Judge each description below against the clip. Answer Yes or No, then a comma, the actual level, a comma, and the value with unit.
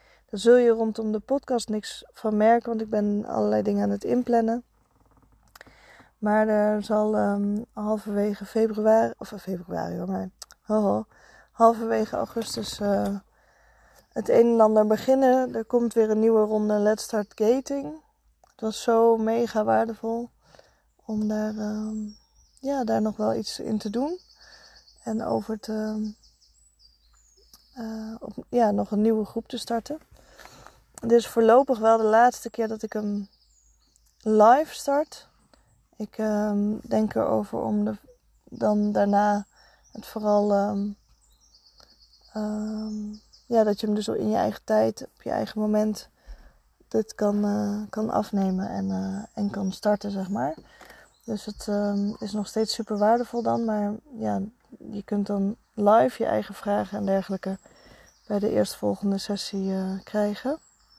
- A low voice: No, high, 215 Hz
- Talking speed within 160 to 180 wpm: No, average, 145 wpm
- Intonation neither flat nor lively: No, narrow, 2.0 semitones